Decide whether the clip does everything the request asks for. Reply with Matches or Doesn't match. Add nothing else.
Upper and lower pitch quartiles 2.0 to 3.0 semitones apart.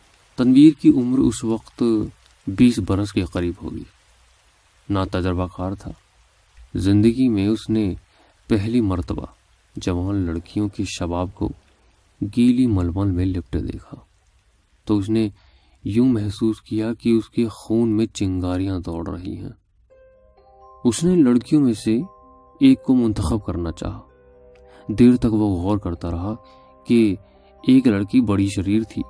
Doesn't match